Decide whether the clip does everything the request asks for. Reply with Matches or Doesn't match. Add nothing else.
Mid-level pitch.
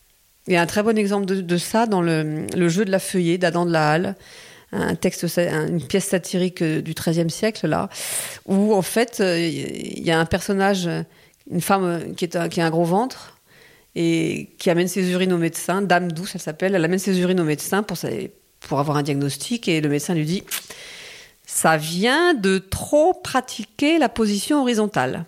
Matches